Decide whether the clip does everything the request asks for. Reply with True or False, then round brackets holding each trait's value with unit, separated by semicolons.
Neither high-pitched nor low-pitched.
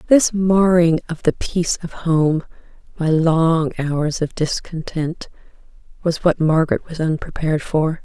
True (165 Hz)